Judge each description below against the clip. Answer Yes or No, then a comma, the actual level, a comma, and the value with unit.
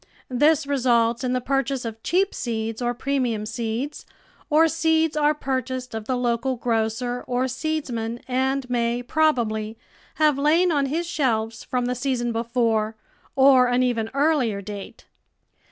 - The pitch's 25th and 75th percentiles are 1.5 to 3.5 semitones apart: Yes, average, 3.2 semitones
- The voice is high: Yes, very high, 250 Hz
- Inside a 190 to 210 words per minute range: No, average, 145 wpm